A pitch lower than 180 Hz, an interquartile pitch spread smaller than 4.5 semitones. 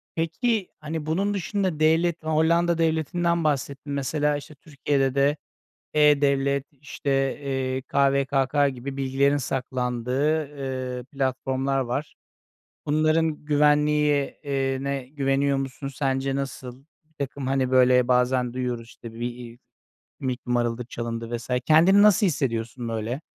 Yes: medium, 140 Hz; average, 2.8 semitones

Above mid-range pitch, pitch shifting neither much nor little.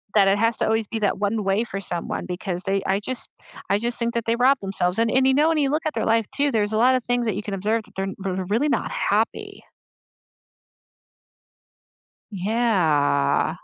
Yes: high, 220 Hz; average, 3.6 semitones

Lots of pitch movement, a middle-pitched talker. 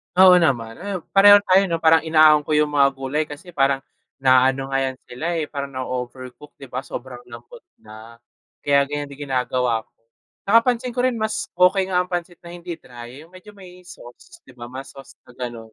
Yes: wide, 5.8 semitones; medium, 145 Hz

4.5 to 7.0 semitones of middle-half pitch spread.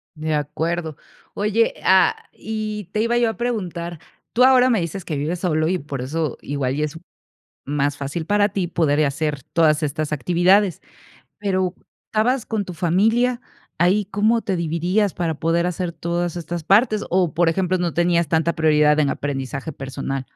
Yes: average, 4.8 semitones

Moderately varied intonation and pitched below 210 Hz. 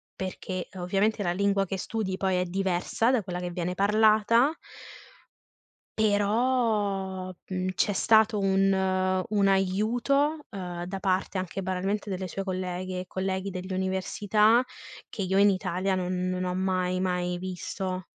No: narrow, 2.0 semitones; high, 190 Hz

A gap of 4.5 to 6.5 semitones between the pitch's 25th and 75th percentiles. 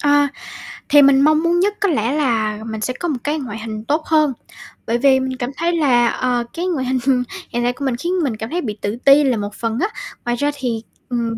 No: average, 4.1 semitones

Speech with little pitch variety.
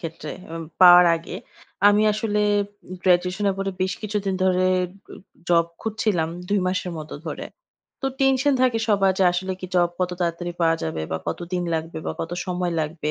No: average, 3.1 semitones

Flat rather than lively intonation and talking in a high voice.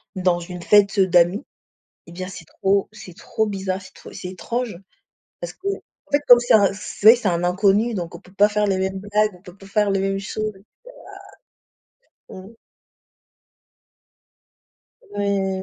Yes: narrow, 2.2 semitones; high, 195 Hz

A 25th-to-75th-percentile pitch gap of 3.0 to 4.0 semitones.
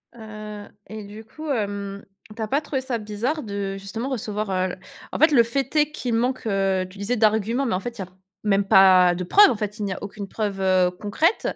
Yes: average, 3.5 semitones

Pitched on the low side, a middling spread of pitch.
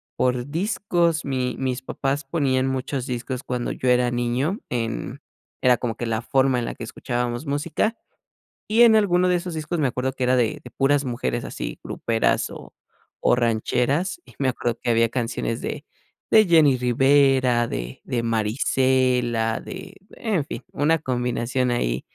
Yes: low, 130 Hz; average, 3.2 semitones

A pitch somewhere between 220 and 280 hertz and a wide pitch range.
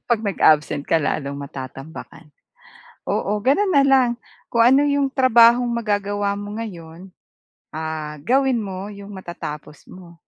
No: high, 200 Hz; wide, 6.9 semitones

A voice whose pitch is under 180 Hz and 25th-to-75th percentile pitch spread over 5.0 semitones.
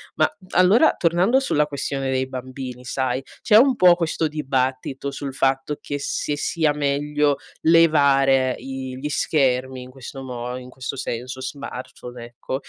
No: low, 135 Hz; narrow, 2.5 semitones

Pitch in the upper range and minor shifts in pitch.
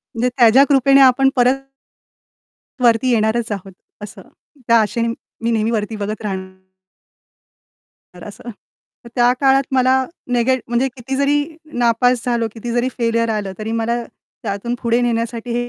Yes: high, 235 Hz; narrow, 2.2 semitones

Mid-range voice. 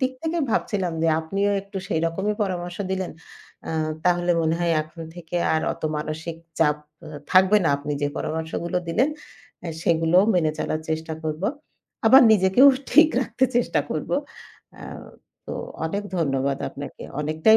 Yes: medium, 170 Hz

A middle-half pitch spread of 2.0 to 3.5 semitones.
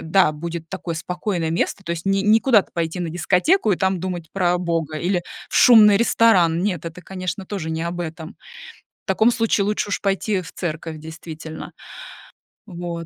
Yes: average, 3.1 semitones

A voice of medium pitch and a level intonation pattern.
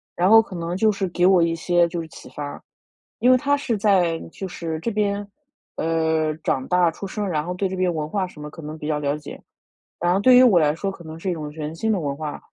No: medium, 175 Hz; average, 3.9 semitones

